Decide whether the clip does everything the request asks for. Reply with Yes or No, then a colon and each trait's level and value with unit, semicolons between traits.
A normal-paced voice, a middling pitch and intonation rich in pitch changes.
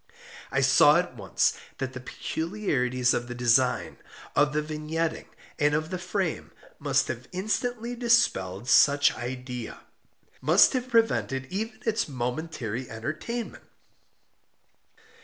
No: slow, 115 wpm; medium, 150 Hz; wide, 7.4 semitones